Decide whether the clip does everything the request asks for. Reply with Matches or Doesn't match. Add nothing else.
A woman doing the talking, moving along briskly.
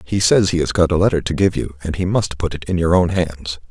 Doesn't match